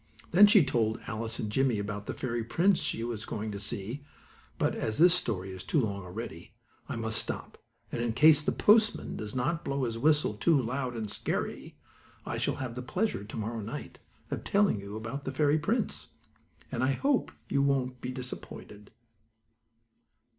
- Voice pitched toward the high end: No, low, 120 Hz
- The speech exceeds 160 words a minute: Yes, average, 180 wpm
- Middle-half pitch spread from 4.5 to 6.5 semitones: Yes, average, 5.1 semitones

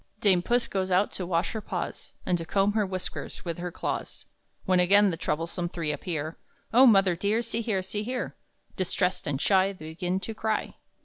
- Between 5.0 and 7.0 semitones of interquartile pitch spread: No, average, 3.1 semitones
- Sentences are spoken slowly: No, average, 195 wpm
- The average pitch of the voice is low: No, medium, 185 Hz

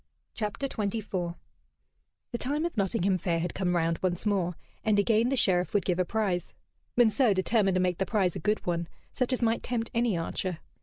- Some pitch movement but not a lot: Yes, average, 4.2 semitones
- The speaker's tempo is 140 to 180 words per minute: No, average, 195 wpm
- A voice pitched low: No, high, 195 Hz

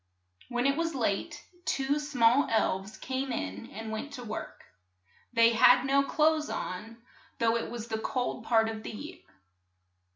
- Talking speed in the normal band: Yes, average, 160 wpm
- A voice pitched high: Yes, high, 235 Hz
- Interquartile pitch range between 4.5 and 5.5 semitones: No, average, 3.7 semitones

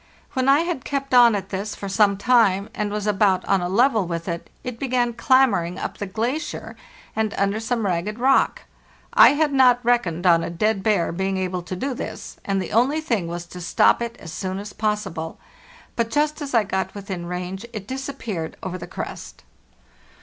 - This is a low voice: No, high, 210 Hz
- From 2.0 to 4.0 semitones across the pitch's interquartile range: No, average, 4.7 semitones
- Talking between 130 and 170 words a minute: No, average, 195 wpm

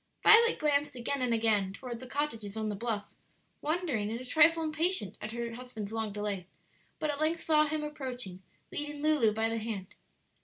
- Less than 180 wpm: No, average, 185 wpm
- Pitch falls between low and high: No, high, 245 Hz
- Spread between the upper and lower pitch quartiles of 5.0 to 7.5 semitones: Yes, wide, 5.6 semitones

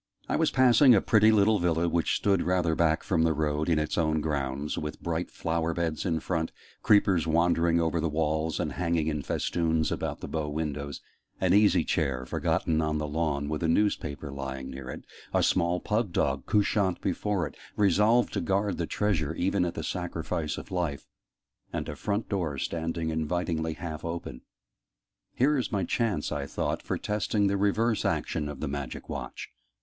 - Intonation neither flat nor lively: Yes, average, 3.8 semitones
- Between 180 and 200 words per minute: Yes, average, 185 wpm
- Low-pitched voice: Yes, very low, 85 Hz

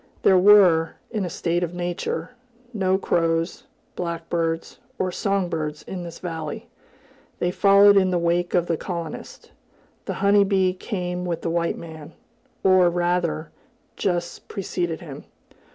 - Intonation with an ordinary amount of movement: No, narrow, 2.0 semitones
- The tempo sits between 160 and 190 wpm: No, average, 140 wpm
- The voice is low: No, medium, 175 Hz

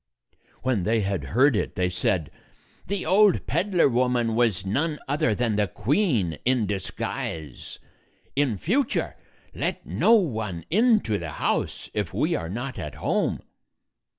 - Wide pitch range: Yes, wide, 7.9 semitones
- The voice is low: Yes, low, 115 Hz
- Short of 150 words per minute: Yes, average, 140 wpm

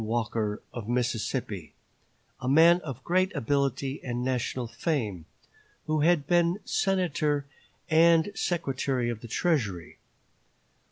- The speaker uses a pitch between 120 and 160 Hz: Yes, low, 135 Hz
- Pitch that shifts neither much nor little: No, wide, 5.8 semitones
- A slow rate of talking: Yes, slow, 110 wpm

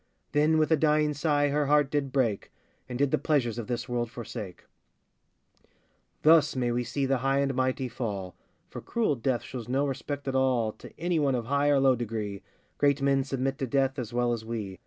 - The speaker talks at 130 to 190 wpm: No, fast, 205 wpm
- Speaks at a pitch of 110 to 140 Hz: Yes, low, 135 Hz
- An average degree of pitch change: Yes, average, 3.2 semitones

